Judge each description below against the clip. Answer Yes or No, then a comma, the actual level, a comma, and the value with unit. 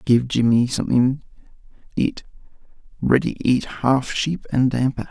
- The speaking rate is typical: No, slow, 120 wpm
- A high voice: No, low, 130 Hz